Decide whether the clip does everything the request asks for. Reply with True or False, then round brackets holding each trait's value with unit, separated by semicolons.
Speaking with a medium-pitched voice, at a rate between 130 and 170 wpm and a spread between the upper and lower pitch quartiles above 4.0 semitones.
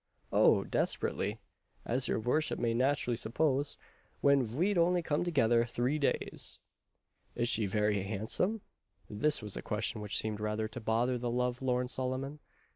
False (125 Hz; 150 wpm; 4.4 semitones)